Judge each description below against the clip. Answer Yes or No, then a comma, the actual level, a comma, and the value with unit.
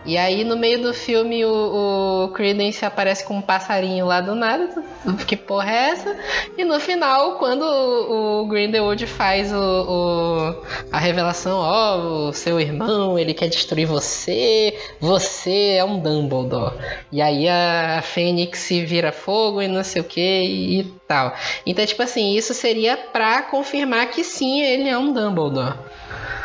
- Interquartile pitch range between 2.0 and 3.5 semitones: No, average, 4.9 semitones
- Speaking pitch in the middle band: No, high, 200 Hz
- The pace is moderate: Yes, average, 160 wpm